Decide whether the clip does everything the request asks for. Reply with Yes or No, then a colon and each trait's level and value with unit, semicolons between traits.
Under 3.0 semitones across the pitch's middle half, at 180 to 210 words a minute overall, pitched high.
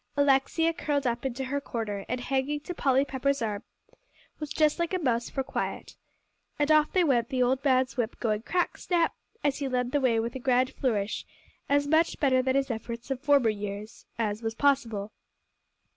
No: average, 3.5 semitones; average, 190 wpm; very high, 260 Hz